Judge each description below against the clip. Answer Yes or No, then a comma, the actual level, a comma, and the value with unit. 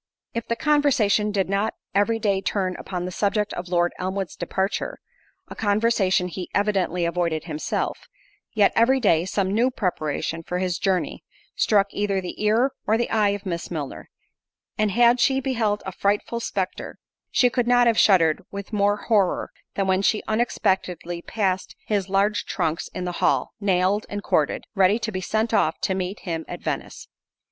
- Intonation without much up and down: No, average, 3.1 semitones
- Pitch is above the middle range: Yes, high, 200 Hz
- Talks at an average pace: Yes, average, 165 wpm